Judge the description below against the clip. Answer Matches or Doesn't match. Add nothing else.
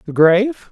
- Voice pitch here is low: Doesn't match